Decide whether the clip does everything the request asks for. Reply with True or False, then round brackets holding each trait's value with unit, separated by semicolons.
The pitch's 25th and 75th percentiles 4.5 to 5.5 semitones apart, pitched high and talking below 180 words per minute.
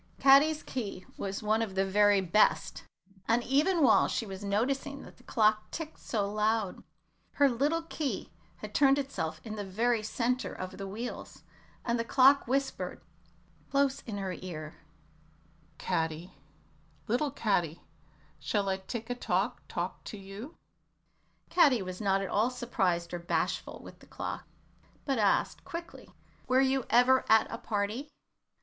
True (5.2 semitones; 225 Hz; 150 wpm)